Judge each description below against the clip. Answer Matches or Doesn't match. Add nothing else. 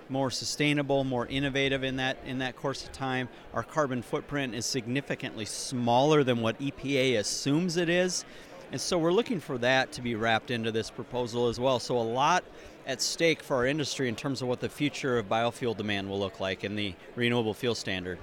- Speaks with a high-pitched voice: Doesn't match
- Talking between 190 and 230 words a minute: Matches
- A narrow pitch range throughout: Doesn't match